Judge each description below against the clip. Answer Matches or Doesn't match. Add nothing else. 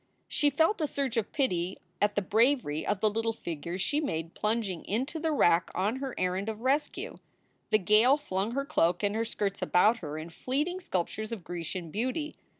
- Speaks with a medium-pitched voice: Doesn't match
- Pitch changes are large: Matches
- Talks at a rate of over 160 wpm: Matches